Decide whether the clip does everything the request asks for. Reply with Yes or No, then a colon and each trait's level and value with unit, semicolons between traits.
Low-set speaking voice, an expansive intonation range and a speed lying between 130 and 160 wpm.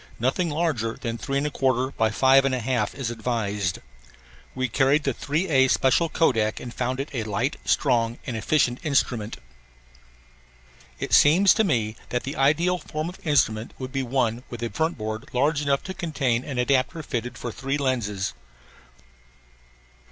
No: low, 130 Hz; average, 3.9 semitones; average, 155 wpm